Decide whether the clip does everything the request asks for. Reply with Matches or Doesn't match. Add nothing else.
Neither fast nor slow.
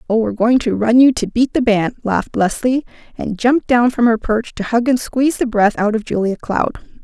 Doesn't match